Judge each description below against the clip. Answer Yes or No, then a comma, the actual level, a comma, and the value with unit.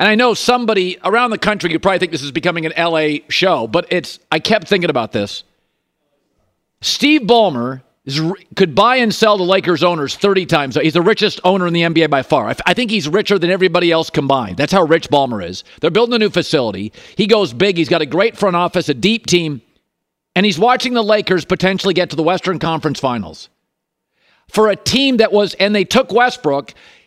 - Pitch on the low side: No, medium, 180 Hz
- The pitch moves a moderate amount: Yes, average, 4.3 semitones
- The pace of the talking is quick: Yes, fast, 210 wpm